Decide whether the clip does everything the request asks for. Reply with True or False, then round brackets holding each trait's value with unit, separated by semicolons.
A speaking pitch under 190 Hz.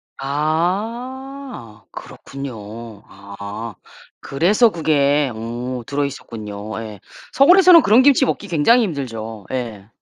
True (140 Hz)